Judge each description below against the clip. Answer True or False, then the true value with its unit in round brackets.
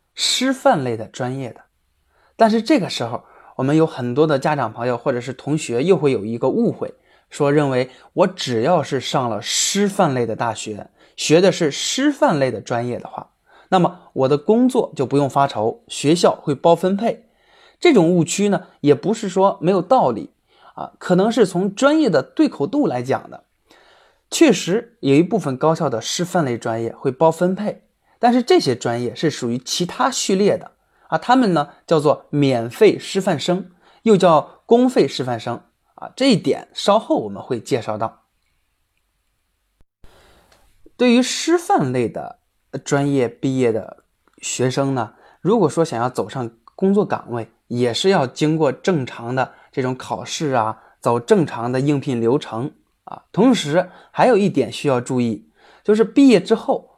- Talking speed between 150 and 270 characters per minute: True (240 characters per minute)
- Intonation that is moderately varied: False (8.4 semitones)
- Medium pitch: True (145 Hz)